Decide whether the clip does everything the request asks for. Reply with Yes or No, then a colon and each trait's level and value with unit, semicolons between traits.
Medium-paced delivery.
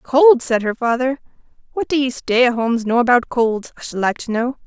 No: fast, 230 wpm